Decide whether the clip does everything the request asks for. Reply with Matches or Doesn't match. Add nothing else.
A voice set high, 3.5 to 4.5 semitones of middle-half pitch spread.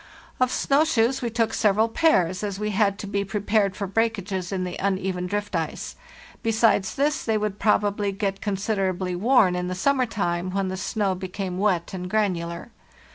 Doesn't match